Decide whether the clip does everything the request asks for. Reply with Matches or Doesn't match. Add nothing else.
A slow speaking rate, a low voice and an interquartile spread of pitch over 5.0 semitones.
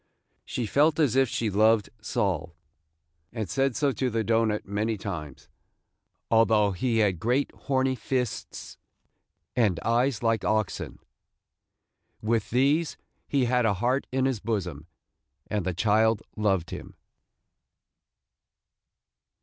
Doesn't match